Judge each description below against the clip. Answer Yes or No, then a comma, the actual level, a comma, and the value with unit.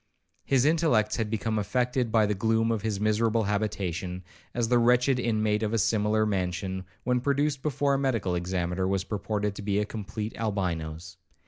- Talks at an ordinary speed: Yes, average, 175 wpm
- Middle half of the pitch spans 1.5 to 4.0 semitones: Yes, average, 3.3 semitones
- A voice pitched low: Yes, low, 110 Hz